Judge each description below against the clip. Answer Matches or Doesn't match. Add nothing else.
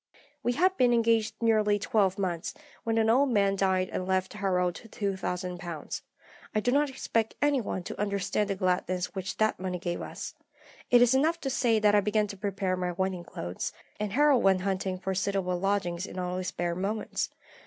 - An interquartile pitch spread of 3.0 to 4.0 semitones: Matches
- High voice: Matches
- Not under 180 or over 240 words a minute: Matches